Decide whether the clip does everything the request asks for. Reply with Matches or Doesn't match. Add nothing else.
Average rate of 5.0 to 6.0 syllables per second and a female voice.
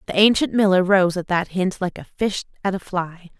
Matches